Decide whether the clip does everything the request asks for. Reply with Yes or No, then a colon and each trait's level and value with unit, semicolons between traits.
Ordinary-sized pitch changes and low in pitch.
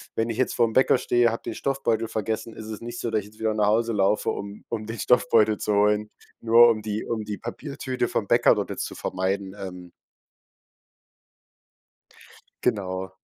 No: narrow, 2.0 semitones; low, 110 Hz